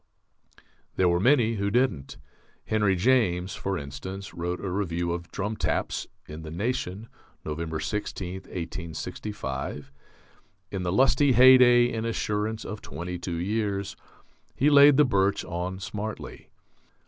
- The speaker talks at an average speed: No, slow, 130 wpm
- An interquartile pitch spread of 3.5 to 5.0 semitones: Yes, average, 4.5 semitones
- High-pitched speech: No, very low, 95 Hz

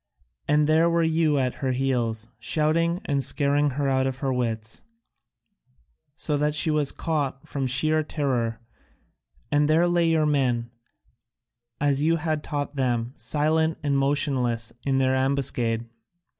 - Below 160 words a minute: Yes, average, 145 wpm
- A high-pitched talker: No, medium, 140 Hz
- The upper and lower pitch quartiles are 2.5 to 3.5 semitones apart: Yes, average, 3.2 semitones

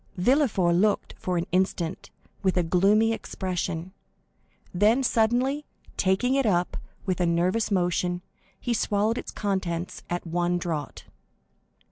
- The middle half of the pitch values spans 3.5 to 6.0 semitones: Yes, average, 3.8 semitones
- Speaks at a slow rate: Yes, slow, 125 wpm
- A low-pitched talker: No, medium, 185 Hz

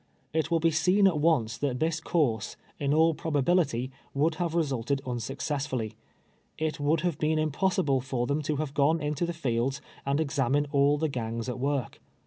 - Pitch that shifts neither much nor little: Yes, average, 3.3 semitones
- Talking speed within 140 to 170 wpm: No, average, 180 wpm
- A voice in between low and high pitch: Yes, medium, 145 Hz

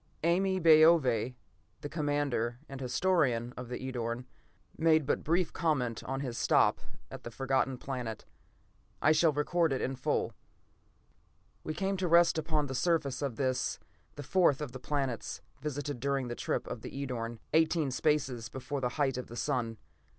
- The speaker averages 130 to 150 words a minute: No, average, 165 wpm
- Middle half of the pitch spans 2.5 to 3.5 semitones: No, average, 3.9 semitones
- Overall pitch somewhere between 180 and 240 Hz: No, medium, 140 Hz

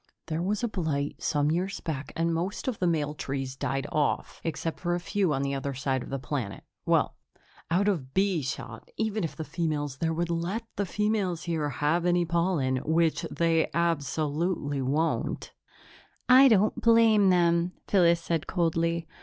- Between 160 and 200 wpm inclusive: Yes, average, 170 wpm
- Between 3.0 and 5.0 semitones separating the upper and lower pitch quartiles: Yes, average, 3.6 semitones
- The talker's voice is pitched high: No, medium, 165 Hz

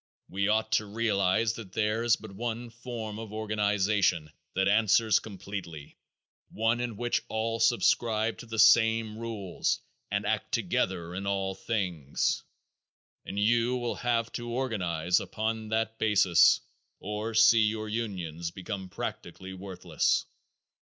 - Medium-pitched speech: No, low, 110 Hz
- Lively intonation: No, average, 2.9 semitones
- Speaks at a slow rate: Yes, slow, 130 wpm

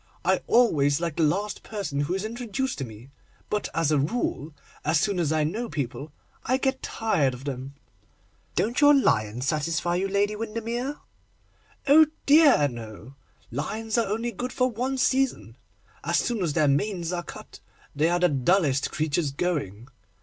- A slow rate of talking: No, average, 165 wpm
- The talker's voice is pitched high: No, medium, 175 Hz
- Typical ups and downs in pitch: No, wide, 8.1 semitones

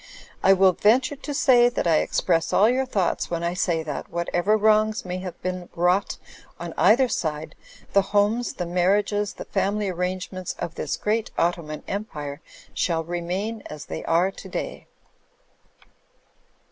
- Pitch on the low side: No, medium, 185 Hz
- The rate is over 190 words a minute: No, average, 155 wpm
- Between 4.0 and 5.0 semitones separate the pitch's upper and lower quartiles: No, average, 3.6 semitones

